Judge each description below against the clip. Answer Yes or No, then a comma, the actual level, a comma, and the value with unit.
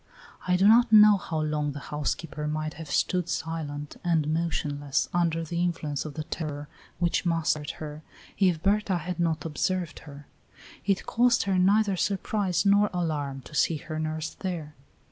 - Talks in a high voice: No, medium, 165 Hz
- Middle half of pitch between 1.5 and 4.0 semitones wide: Yes, average, 3.4 semitones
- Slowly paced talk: No, average, 165 wpm